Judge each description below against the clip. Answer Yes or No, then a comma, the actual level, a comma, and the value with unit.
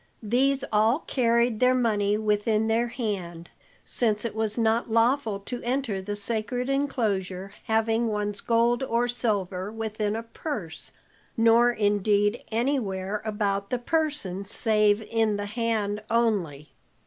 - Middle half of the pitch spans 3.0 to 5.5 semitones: No, narrow, 2.5 semitones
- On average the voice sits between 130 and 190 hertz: No, high, 220 Hz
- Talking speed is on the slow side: Yes, slow, 130 wpm